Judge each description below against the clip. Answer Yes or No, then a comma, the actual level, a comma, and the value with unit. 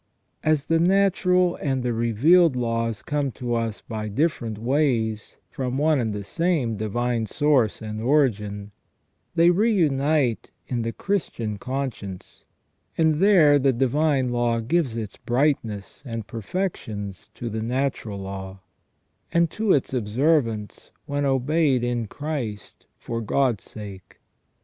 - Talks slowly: Yes, slow, 130 wpm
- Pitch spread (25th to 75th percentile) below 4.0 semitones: No, average, 5.3 semitones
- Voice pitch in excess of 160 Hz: No, low, 125 Hz